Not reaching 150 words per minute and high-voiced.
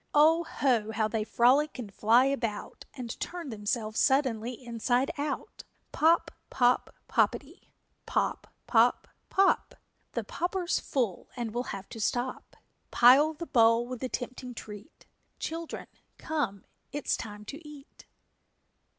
Yes: slow, 135 wpm; very high, 250 Hz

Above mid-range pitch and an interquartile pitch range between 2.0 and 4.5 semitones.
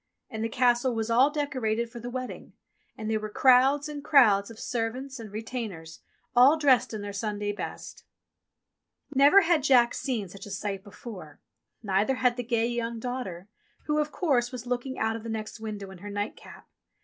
Yes: high, 235 Hz; average, 3.5 semitones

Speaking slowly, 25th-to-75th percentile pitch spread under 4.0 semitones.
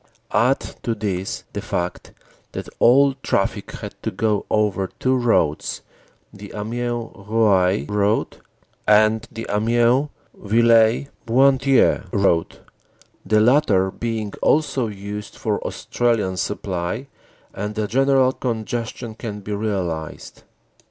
Yes: slow, 110 wpm; average, 2.9 semitones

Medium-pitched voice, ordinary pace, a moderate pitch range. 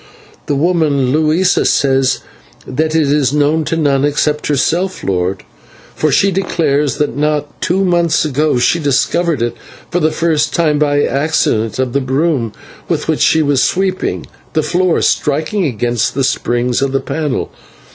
Yes: medium, 150 Hz; average, 160 wpm; average, 3.0 semitones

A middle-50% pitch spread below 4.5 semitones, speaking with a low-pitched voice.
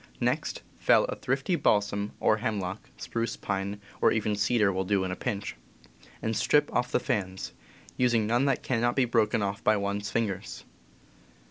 Yes: average, 2.9 semitones; low, 105 Hz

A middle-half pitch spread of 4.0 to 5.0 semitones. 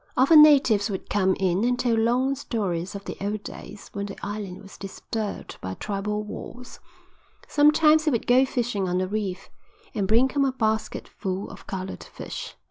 Yes: average, 4.3 semitones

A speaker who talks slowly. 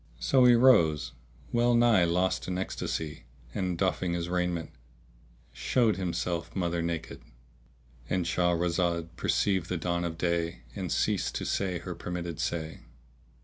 Yes: slow, 130 wpm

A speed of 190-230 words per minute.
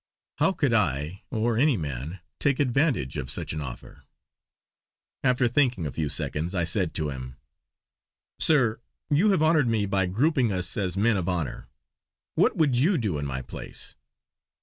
No: average, 165 wpm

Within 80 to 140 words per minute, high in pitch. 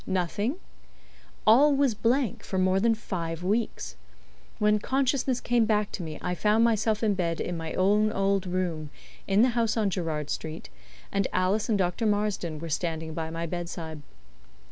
No: average, 165 wpm; high, 195 Hz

